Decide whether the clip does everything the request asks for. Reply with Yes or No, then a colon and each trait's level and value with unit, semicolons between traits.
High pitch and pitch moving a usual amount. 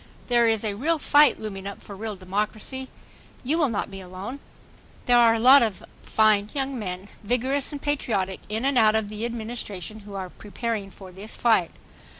Yes: high, 220 Hz; average, 3.6 semitones